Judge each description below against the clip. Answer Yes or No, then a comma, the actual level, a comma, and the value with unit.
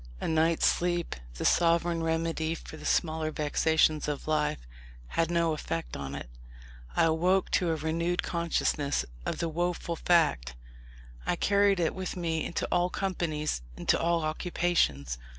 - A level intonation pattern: Yes, narrow, 1.9 semitones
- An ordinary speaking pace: Yes, average, 150 wpm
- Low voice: No, medium, 165 Hz